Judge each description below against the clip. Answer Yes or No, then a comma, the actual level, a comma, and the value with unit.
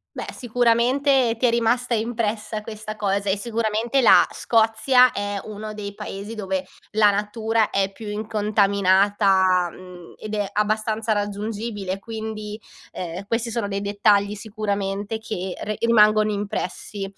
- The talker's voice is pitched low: No, high, 210 Hz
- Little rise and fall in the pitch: Yes, narrow, 1.9 semitones